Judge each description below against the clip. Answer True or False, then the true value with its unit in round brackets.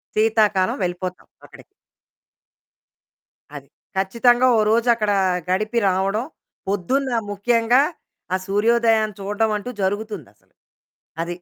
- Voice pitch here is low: False (215 Hz)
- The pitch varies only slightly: False (3.2 semitones)